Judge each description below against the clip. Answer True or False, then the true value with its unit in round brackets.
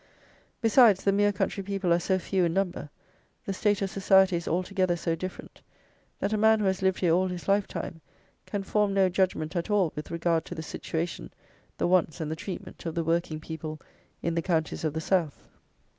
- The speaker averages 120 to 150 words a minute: False (205 wpm)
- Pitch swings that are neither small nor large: True (3.0 semitones)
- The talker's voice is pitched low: False (185 Hz)